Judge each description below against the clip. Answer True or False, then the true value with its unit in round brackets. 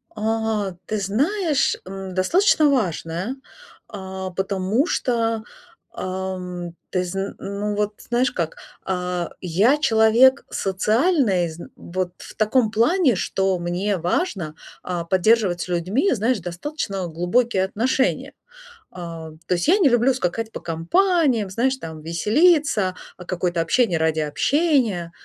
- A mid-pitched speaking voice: False (195 Hz)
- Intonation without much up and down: False (5.6 semitones)